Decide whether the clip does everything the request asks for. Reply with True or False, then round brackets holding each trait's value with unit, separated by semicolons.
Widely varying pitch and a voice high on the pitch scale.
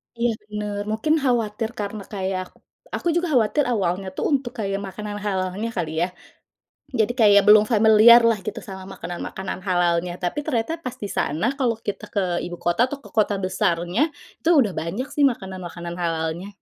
False (3.8 semitones; 205 Hz)